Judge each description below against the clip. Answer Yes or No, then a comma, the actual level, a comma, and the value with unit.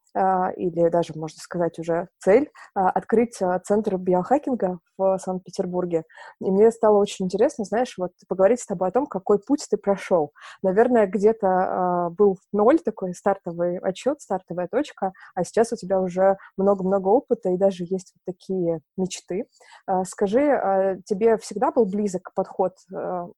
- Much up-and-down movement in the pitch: No, average, 2.9 semitones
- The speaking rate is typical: Yes, average, 145 wpm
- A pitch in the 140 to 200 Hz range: Yes, high, 190 Hz